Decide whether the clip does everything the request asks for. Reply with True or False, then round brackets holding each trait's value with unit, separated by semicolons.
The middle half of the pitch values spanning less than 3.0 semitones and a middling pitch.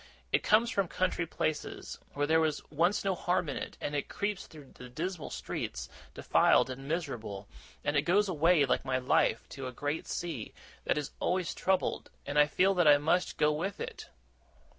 False (4.1 semitones; 155 Hz)